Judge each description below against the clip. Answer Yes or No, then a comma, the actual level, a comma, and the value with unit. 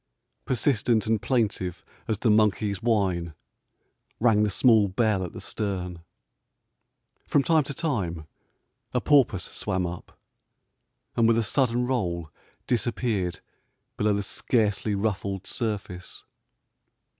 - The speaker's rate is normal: No, slow, 115 wpm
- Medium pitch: No, low, 105 Hz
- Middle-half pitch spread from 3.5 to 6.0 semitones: Yes, average, 4.0 semitones